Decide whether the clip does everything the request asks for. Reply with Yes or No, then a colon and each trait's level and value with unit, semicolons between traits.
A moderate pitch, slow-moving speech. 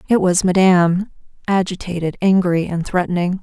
Yes: medium, 180 Hz; slow, 125 wpm